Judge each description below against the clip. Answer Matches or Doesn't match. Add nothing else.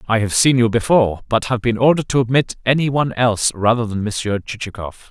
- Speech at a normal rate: Doesn't match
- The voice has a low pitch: Matches